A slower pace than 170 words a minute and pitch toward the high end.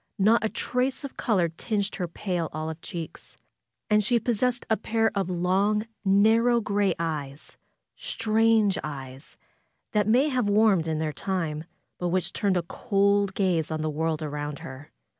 Yes: average, 160 wpm; high, 195 Hz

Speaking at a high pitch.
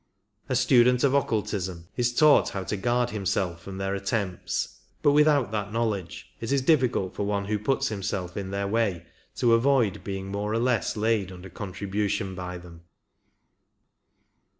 No: low, 105 Hz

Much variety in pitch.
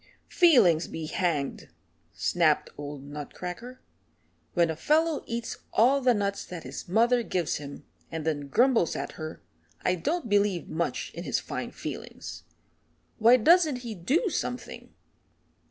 Yes: wide, 7.5 semitones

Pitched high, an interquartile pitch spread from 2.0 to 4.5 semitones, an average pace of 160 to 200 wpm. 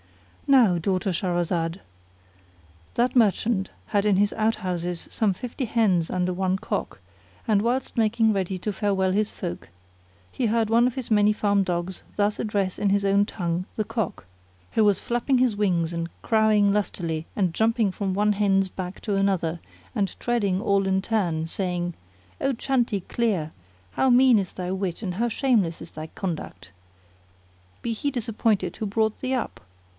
Yes: high, 200 Hz; average, 3.5 semitones; average, 165 wpm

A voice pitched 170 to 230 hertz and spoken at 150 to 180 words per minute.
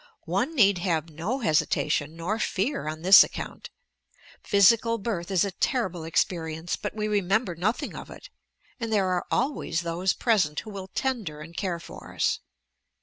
Yes: high, 190 Hz; average, 160 wpm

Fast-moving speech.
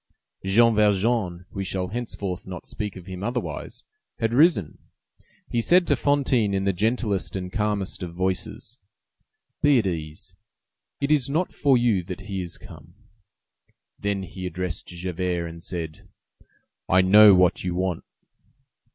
No: average, 140 wpm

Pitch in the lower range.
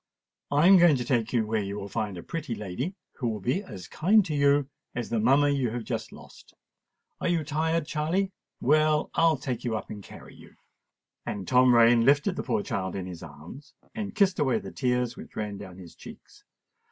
Yes: low, 125 Hz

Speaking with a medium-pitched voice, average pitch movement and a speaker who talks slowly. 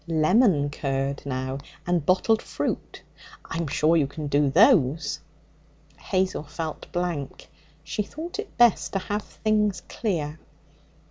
No: medium, 165 Hz; wide, 6.0 semitones; slow, 125 wpm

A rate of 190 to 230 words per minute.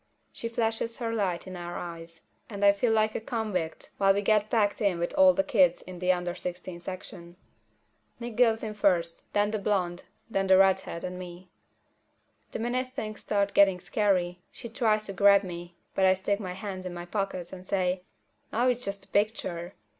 Yes: average, 195 wpm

